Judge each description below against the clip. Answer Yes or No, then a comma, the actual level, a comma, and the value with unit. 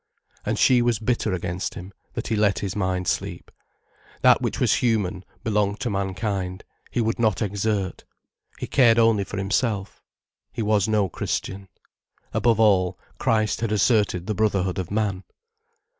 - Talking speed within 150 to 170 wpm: Yes, average, 155 wpm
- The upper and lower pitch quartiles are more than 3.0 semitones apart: No, narrow, 2.6 semitones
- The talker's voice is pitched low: Yes, low, 105 Hz